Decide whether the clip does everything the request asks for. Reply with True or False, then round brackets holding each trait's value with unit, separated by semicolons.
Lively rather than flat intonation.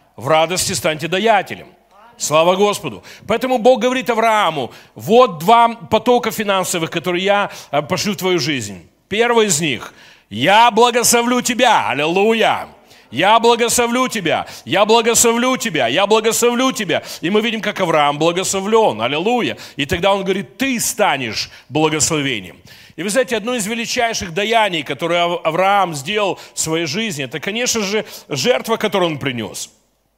True (6.1 semitones)